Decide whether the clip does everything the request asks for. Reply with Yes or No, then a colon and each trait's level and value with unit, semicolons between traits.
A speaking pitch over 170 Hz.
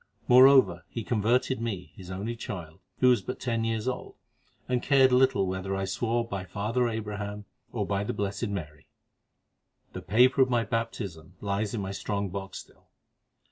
No: low, 105 Hz